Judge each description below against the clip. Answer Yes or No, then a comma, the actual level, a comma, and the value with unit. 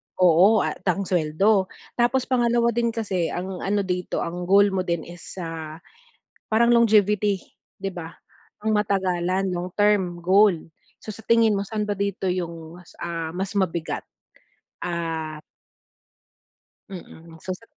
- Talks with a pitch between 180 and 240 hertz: Yes, high, 190 Hz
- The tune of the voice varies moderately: Yes, average, 3.3 semitones